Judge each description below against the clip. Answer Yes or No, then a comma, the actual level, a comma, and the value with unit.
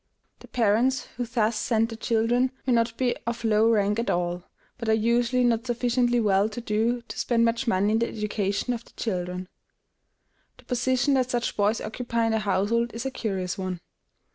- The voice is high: Yes, high, 230 Hz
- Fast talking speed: No, average, 190 wpm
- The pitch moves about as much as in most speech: No, narrow, 2.3 semitones